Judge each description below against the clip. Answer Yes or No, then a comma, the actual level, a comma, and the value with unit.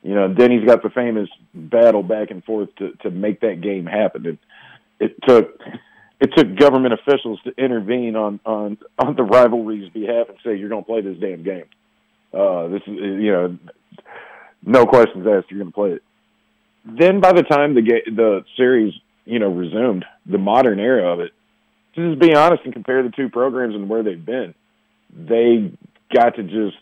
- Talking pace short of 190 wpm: No, average, 195 wpm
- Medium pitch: No, low, 115 Hz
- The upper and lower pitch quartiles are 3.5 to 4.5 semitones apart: Yes, average, 4.1 semitones